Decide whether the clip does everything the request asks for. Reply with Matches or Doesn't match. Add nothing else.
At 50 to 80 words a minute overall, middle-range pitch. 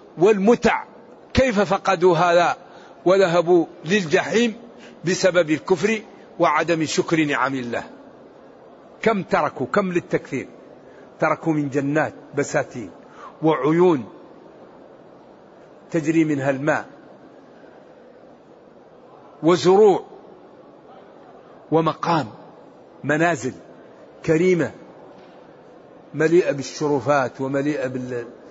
Matches